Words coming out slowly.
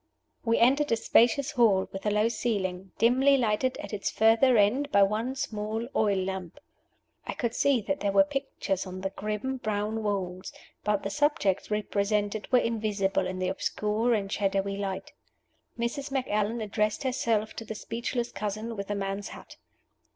No: average, 165 wpm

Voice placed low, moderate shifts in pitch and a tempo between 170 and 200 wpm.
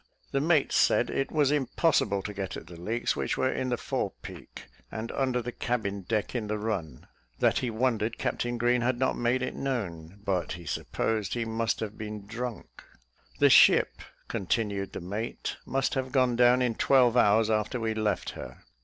Yes: low, 115 Hz; average, 3.4 semitones; average, 190 wpm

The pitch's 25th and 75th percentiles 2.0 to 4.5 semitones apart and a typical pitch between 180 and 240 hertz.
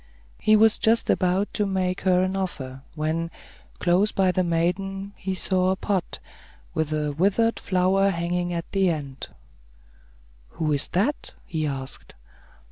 Yes: average, 2.8 semitones; medium, 185 Hz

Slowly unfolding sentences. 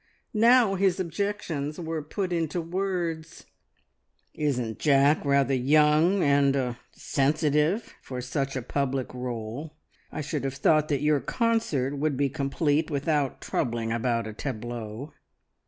Yes: slow, 130 wpm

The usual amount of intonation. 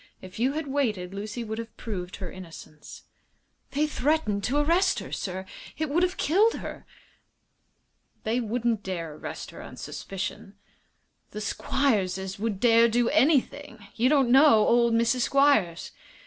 No: wide, 5.9 semitones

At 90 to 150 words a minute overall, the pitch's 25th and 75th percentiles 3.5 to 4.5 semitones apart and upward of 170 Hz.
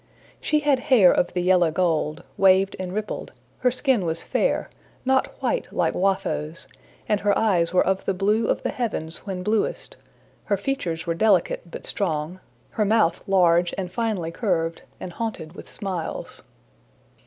No: average, 160 wpm; average, 4.1 semitones; high, 190 Hz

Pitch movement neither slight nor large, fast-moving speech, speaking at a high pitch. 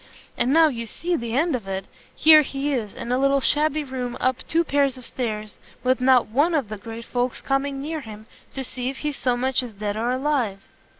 Yes: average, 3.4 semitones; fast, 225 wpm; very high, 255 Hz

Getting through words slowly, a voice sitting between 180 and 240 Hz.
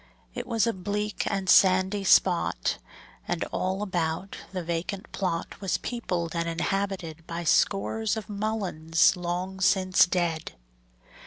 Yes: slow, 130 wpm; medium, 185 Hz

